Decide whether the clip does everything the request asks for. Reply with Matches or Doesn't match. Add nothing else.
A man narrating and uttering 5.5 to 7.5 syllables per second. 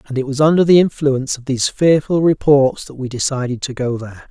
Matches